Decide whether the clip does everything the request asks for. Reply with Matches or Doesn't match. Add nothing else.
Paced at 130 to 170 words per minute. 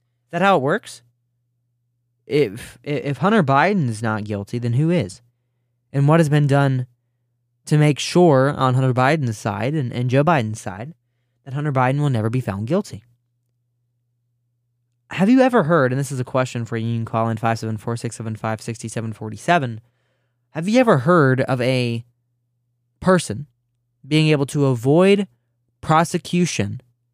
Matches